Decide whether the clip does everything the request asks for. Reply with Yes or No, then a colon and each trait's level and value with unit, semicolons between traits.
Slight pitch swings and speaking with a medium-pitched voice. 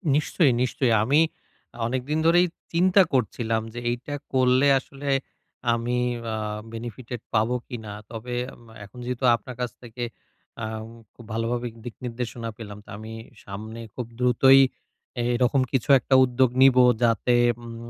No: narrow, 2.2 semitones; low, 125 Hz